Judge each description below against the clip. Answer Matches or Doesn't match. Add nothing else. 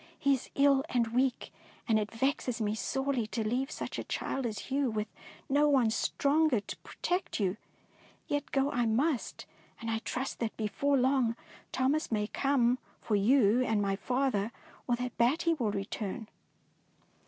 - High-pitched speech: Matches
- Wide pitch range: Doesn't match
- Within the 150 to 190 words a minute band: Matches